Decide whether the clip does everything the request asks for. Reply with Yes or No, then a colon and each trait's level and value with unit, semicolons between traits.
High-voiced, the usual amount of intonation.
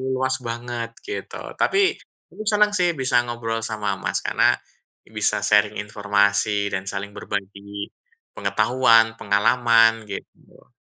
No: low, 115 Hz; average, 3.5 semitones